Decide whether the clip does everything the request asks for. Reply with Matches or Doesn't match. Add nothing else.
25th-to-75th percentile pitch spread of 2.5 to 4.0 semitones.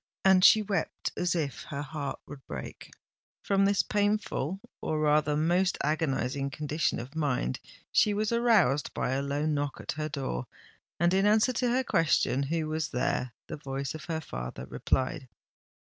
Doesn't match